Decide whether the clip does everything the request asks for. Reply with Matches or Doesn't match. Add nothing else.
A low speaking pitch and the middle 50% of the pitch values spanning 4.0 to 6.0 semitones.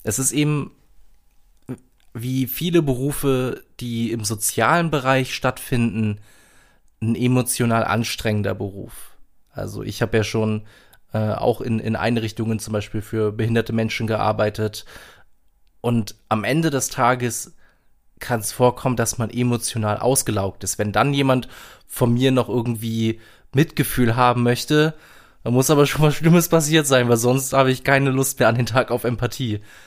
Doesn't match